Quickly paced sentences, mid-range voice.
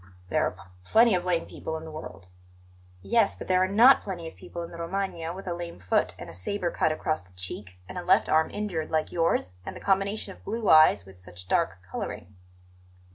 Yes: fast, 225 wpm; medium, 165 Hz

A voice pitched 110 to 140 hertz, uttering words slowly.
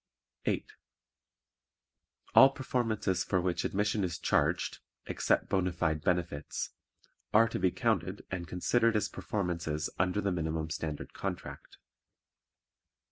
No: very low, 90 Hz; slow, 115 wpm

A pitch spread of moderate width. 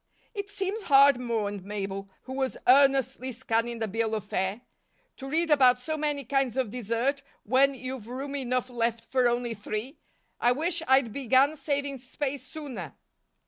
Yes: average, 3.4 semitones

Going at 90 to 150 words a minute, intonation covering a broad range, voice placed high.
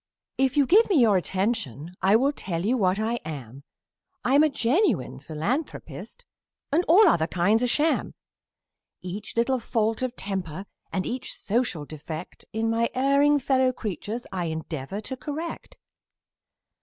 Yes: average, 145 wpm; wide, 6.7 semitones; high, 225 Hz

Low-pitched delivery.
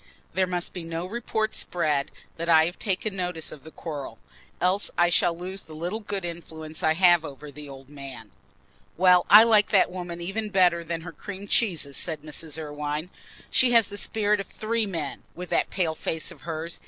No: medium, 175 Hz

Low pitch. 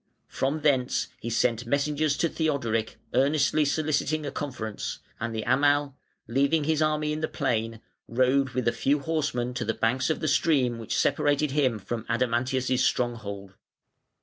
Yes: low, 130 Hz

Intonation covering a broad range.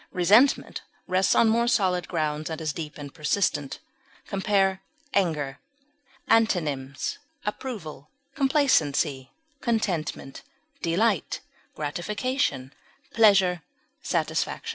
Yes: wide, 6.5 semitones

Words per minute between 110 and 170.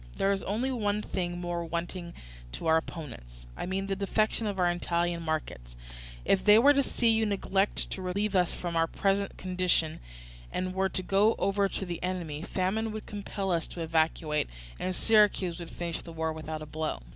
No: average, 190 wpm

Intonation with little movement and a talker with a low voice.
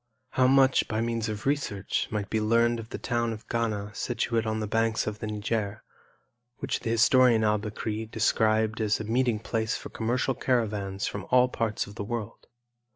Yes: narrow, 1.7 semitones; low, 110 Hz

